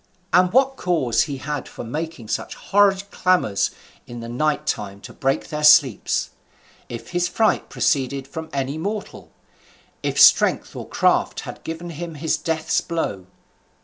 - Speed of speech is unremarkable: Yes, average, 150 wpm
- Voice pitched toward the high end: No, medium, 155 Hz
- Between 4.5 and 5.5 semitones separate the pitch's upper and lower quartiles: Yes, average, 4.9 semitones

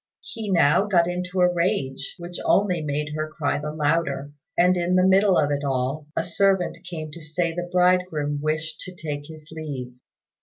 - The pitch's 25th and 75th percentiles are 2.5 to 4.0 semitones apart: Yes, average, 3.5 semitones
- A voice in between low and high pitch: Yes, medium, 165 Hz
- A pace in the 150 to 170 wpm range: No, average, 185 wpm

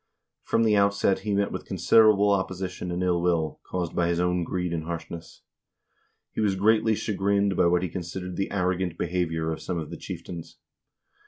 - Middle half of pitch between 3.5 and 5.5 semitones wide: No, average, 2.7 semitones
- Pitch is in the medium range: No, very low, 90 Hz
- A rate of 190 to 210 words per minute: No, average, 180 wpm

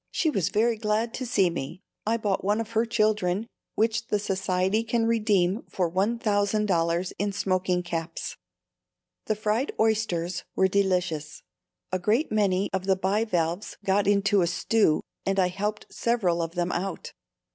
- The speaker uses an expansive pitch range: No, average, 3.1 semitones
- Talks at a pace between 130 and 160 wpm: Yes, average, 155 wpm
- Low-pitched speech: No, high, 200 Hz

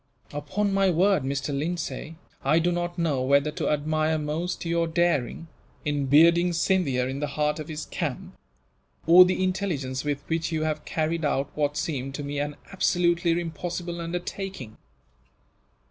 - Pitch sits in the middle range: Yes, medium, 160 Hz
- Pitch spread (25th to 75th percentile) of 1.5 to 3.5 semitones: Yes, average, 3.1 semitones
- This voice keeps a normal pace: Yes, average, 155 wpm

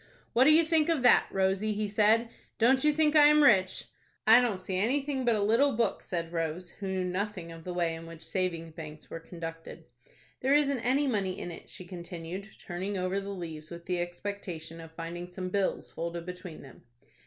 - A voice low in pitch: No, high, 190 Hz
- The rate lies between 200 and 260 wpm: Yes, fast, 205 wpm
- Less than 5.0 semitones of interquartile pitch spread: No, average, 5.3 semitones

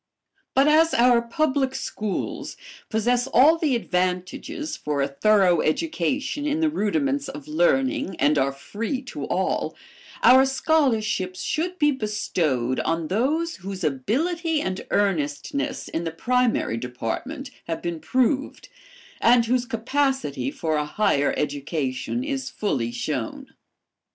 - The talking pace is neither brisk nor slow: No, slow, 125 wpm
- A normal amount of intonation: No, wide, 9.0 semitones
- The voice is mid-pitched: No, high, 225 Hz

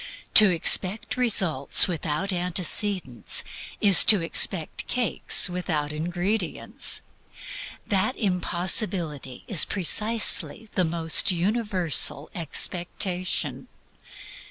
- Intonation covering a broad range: No, average, 3.7 semitones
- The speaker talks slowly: Yes, slow, 80 wpm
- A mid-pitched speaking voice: Yes, medium, 180 Hz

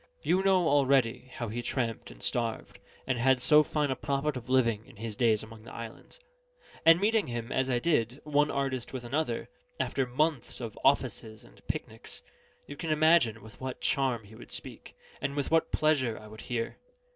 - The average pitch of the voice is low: Yes, low, 130 Hz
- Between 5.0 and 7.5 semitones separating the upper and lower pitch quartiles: No, average, 4.3 semitones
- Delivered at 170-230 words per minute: Yes, average, 190 wpm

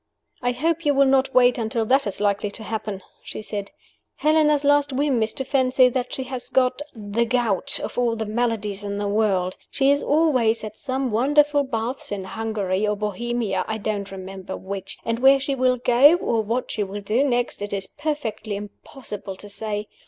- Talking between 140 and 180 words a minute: No, average, 195 wpm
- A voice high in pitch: Yes, high, 230 Hz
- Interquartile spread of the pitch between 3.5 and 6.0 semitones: Yes, average, 4.3 semitones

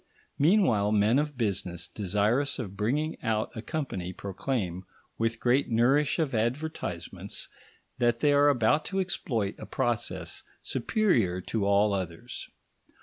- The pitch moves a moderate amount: No, wide, 6.2 semitones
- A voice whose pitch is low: Yes, low, 115 Hz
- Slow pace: Yes, slow, 130 wpm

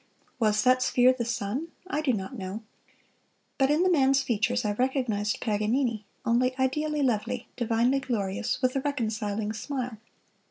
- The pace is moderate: Yes, average, 150 wpm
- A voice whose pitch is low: No, high, 245 Hz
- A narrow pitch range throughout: No, average, 3.6 semitones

